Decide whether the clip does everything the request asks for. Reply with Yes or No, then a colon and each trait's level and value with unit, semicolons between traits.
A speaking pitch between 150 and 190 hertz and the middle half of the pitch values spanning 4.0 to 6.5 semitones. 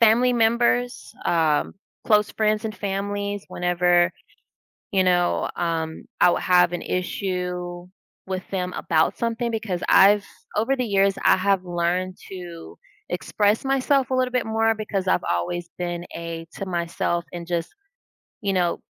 No: medium, 185 Hz; average, 3.6 semitones